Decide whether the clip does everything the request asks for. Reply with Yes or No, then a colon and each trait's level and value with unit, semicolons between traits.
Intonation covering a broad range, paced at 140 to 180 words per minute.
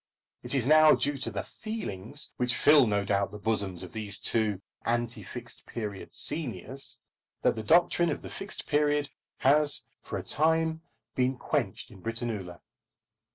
Yes: wide, 6.1 semitones; average, 155 wpm